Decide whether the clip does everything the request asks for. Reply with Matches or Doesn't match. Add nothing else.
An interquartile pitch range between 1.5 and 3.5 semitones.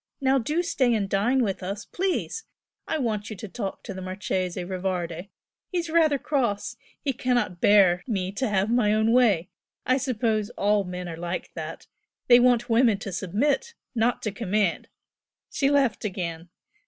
Doesn't match